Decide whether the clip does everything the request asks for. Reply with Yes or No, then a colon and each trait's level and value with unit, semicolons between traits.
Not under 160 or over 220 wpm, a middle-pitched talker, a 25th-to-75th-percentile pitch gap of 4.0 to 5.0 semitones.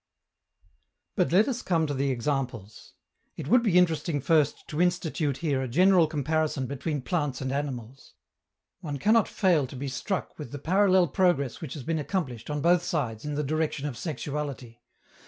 Yes: average, 175 wpm; medium, 150 Hz; average, 4.3 semitones